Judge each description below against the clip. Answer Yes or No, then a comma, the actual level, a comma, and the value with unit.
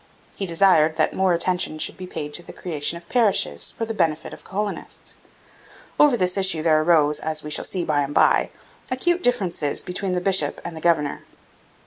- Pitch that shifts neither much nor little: Yes, average, 3.8 semitones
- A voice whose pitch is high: No, medium, 175 Hz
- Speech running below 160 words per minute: No, average, 195 wpm